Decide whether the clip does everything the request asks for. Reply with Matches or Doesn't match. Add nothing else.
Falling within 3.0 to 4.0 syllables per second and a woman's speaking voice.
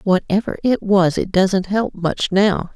Matches